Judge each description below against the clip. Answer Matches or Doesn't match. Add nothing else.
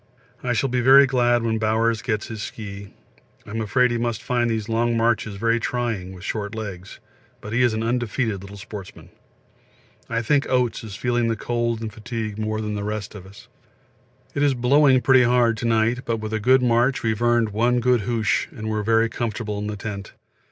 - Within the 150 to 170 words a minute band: Doesn't match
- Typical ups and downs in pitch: Doesn't match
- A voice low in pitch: Matches